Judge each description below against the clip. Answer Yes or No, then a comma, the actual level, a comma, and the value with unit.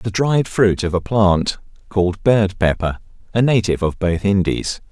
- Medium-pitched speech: No, low, 100 Hz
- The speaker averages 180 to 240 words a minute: No, average, 170 wpm